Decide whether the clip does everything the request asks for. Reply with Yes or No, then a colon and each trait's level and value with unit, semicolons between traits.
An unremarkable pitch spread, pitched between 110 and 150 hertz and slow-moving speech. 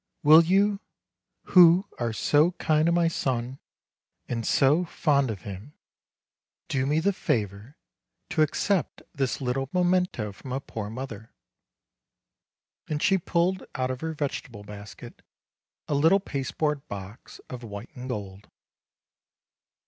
No: wide, 6.2 semitones; medium, 140 Hz; slow, 130 wpm